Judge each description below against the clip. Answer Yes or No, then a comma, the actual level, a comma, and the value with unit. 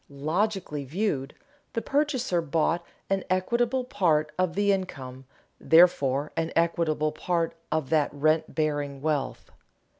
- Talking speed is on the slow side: Yes, slow, 120 wpm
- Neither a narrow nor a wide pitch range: Yes, average, 4.2 semitones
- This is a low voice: No, medium, 165 Hz